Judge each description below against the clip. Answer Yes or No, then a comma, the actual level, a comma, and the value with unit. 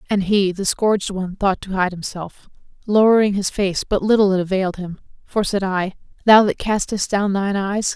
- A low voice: No, high, 195 Hz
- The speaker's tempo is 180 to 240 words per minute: Yes, average, 195 wpm